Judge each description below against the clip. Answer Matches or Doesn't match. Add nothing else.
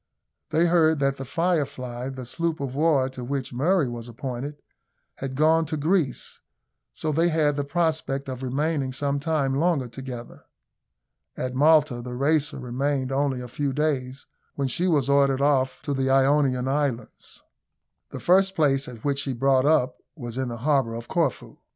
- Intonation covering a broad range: Doesn't match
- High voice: Doesn't match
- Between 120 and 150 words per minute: Doesn't match